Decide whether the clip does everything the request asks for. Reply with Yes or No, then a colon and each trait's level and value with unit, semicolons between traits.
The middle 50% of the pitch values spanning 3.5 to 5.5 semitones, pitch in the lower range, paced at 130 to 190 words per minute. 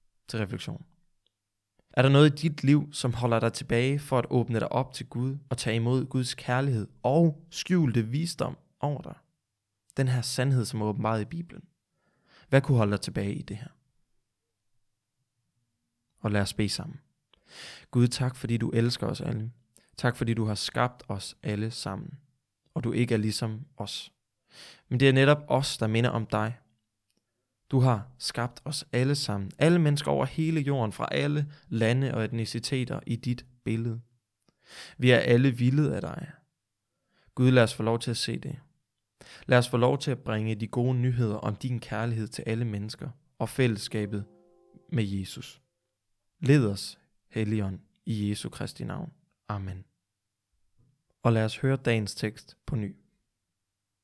Yes: average, 3.8 semitones; low, 120 Hz; average, 165 wpm